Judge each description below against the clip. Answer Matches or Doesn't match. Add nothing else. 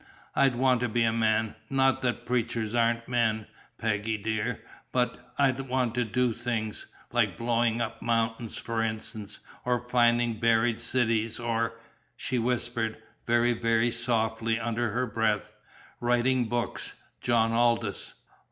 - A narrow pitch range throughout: Matches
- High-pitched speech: Doesn't match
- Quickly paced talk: Doesn't match